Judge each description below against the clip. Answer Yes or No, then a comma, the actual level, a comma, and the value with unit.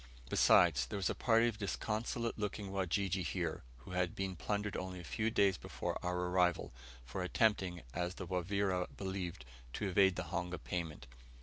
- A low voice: Yes, very low, 95 Hz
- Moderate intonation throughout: No, narrow, 2.3 semitones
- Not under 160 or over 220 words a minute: Yes, average, 170 wpm